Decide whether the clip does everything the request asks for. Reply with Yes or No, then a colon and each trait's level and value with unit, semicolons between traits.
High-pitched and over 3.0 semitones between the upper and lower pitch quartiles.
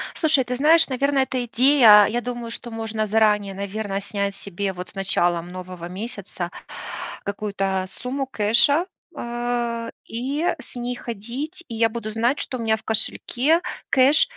Yes: high, 230 Hz; average, 4.0 semitones